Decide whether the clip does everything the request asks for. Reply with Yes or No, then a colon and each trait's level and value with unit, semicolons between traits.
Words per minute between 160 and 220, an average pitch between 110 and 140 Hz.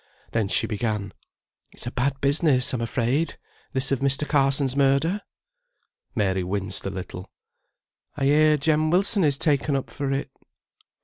No: average, 145 wpm; low, 135 Hz